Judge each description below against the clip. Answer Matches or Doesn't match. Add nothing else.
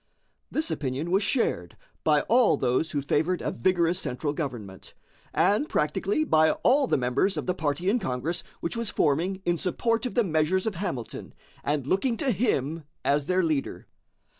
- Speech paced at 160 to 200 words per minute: Matches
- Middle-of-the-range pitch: Matches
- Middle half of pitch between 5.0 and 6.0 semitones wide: Matches